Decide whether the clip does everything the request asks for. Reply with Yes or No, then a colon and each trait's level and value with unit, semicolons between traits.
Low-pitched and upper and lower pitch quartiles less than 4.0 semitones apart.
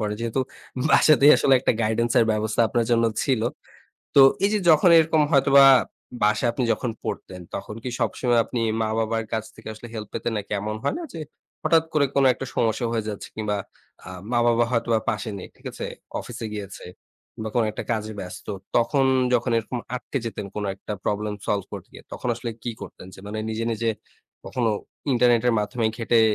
Yes: low, 115 Hz; narrow, 2.5 semitones